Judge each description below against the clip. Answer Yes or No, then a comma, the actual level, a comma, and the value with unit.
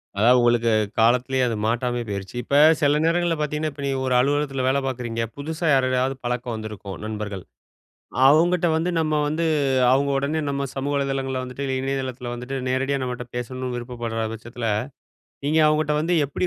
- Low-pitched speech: Yes, low, 130 Hz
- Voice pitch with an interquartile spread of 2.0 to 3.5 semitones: Yes, average, 2.9 semitones